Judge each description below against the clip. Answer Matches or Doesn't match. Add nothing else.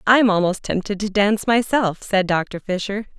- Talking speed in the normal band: Matches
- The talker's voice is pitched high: Matches